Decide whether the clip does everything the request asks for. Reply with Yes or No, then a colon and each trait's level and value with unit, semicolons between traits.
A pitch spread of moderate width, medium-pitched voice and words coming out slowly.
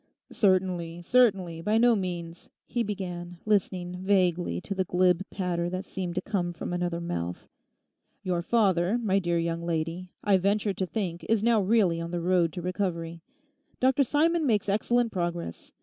No: average, 3.1 semitones; medium, 180 Hz; average, 165 wpm